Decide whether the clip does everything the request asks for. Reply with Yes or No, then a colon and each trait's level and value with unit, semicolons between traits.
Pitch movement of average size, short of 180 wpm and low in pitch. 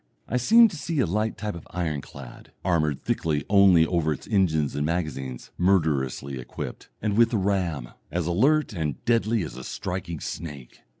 No: wide, 5.8 semitones; average, 170 wpm; very low, 85 Hz